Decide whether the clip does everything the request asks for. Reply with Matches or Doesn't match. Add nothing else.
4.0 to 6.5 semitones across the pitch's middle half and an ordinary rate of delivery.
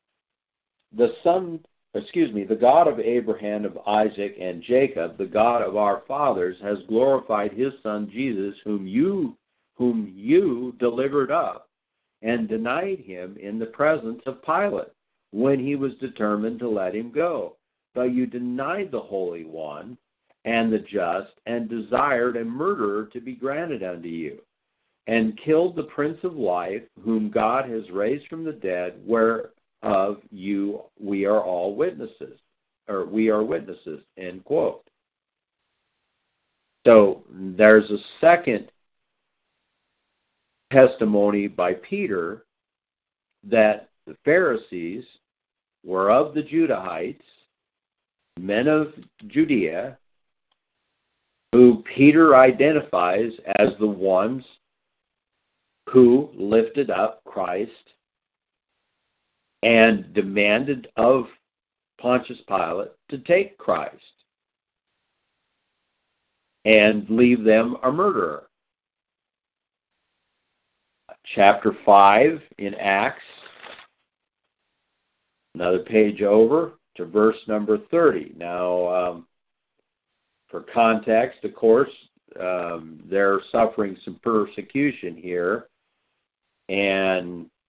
Doesn't match